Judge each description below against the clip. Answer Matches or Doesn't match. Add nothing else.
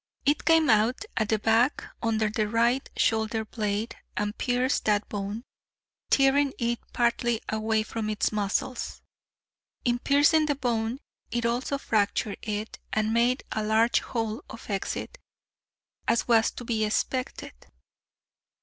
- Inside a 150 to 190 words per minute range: Doesn't match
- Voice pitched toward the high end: Matches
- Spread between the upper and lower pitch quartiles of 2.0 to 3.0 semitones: Matches